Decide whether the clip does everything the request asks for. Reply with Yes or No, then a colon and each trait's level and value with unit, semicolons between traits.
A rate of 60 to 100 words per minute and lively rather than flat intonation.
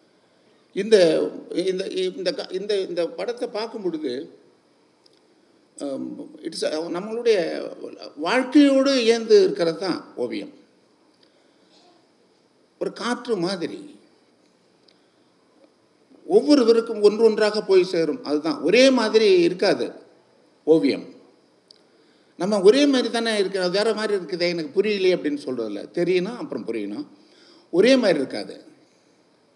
Yes: average, 85 wpm; wide, 7.8 semitones